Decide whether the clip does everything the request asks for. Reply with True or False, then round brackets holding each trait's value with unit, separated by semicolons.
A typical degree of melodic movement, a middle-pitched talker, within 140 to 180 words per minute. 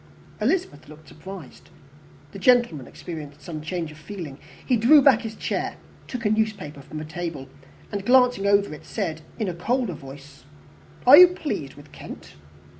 False (7.4 semitones; 180 Hz; 165 wpm)